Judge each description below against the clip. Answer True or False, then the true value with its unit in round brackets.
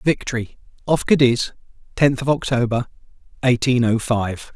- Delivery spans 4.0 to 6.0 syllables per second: True (4.7 syllables/s)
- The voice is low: True (125 Hz)